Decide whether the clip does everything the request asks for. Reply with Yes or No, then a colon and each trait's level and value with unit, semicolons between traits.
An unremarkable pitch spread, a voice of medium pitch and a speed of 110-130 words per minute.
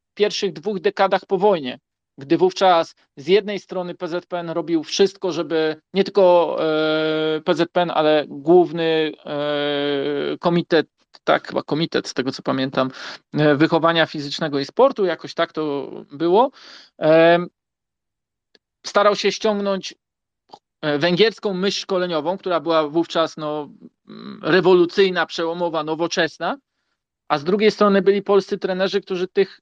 Yes: average, 3.9 semitones; medium, 170 Hz; average, 115 wpm